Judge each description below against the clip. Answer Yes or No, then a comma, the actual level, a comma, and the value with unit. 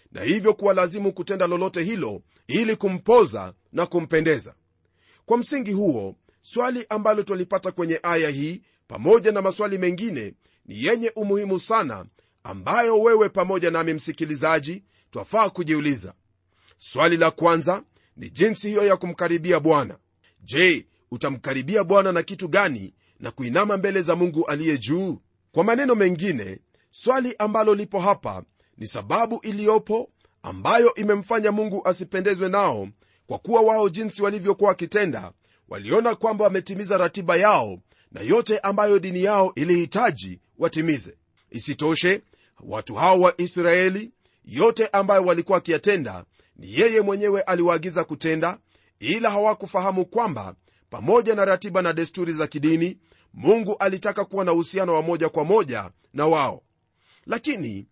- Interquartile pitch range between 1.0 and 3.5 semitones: No, average, 4.6 semitones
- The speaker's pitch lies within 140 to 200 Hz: Yes, medium, 185 Hz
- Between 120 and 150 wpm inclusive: Yes, average, 130 wpm